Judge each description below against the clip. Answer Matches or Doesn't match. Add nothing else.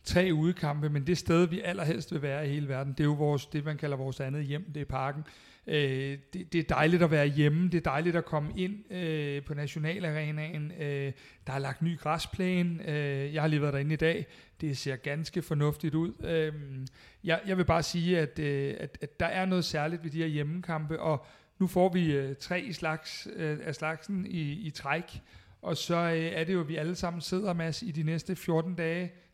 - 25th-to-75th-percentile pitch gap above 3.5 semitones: Doesn't match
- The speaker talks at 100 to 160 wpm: Doesn't match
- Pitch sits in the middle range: Matches